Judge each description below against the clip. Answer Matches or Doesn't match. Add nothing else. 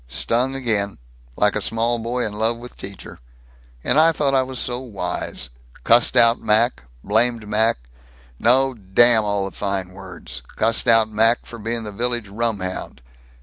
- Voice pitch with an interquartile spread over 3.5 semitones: Doesn't match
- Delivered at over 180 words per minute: Doesn't match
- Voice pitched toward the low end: Matches